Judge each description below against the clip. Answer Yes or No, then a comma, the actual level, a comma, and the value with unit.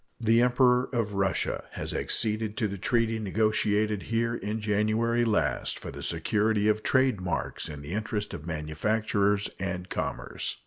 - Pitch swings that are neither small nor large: No, narrow, 2.2 semitones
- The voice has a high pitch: No, low, 110 Hz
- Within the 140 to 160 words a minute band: Yes, average, 150 wpm